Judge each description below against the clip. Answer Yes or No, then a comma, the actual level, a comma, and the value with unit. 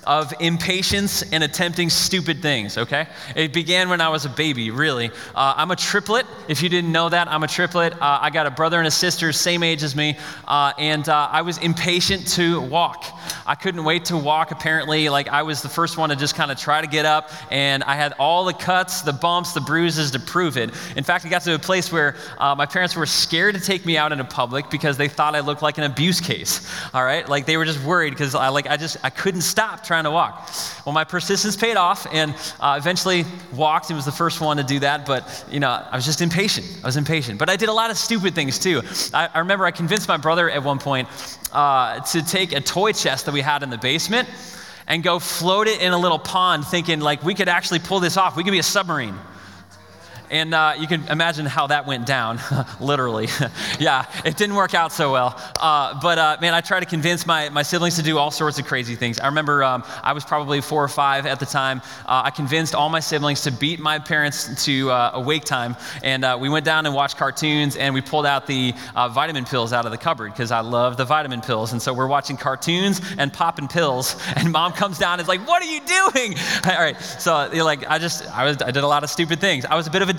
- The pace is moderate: No, fast, 250 wpm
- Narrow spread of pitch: No, average, 3.5 semitones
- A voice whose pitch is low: No, medium, 155 Hz